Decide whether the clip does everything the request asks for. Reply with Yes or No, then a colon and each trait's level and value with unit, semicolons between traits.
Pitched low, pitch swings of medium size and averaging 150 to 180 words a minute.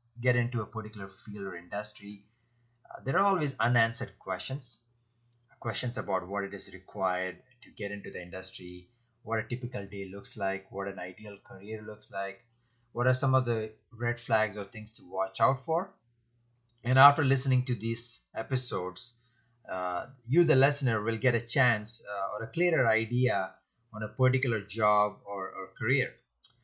Yes: low, 115 Hz; average, 3.3 semitones; average, 170 wpm